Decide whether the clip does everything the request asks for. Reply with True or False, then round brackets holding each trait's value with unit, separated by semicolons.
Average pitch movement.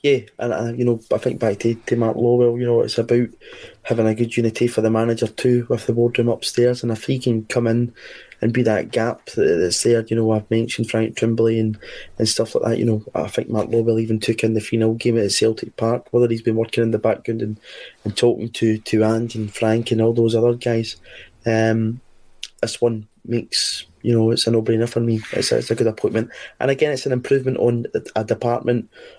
False (1.2 semitones)